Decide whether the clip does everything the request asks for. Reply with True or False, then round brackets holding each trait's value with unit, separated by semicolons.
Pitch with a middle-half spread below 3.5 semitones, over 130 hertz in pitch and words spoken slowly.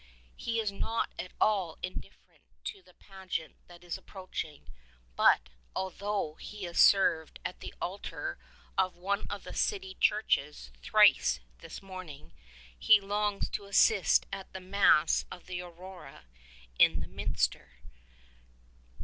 True (3.0 semitones; 190 Hz; 130 wpm)